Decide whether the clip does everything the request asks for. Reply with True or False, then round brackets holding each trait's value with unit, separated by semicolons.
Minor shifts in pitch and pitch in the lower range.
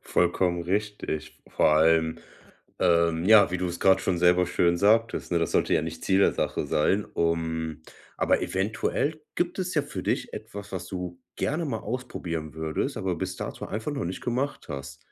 False (4.0 semitones; 90 Hz)